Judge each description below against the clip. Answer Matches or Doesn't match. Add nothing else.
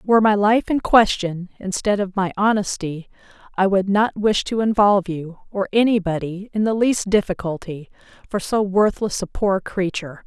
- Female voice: Matches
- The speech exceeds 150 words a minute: Matches